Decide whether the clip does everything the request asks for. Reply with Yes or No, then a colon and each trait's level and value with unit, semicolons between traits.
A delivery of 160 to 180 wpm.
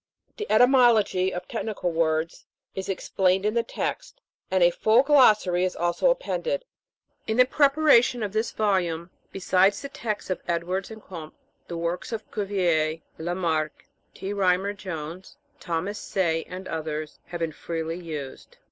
No: average, 150 wpm